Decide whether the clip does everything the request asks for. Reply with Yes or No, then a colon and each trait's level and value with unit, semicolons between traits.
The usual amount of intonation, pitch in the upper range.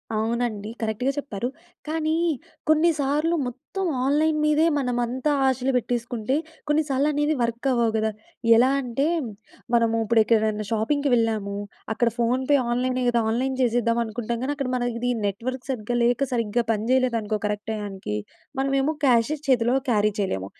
Yes: average, 3.5 semitones; high, 245 Hz